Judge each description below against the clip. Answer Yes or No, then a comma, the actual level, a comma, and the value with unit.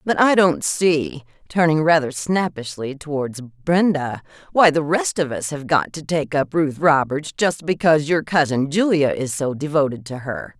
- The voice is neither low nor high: Yes, medium, 150 Hz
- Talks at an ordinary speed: Yes, average, 175 wpm